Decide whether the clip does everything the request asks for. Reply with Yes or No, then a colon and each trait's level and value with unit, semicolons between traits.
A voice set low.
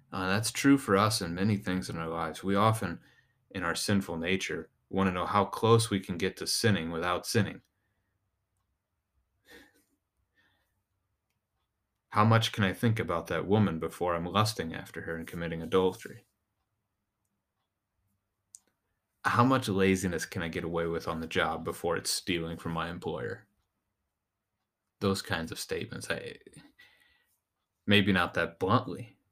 Yes: very low, 95 Hz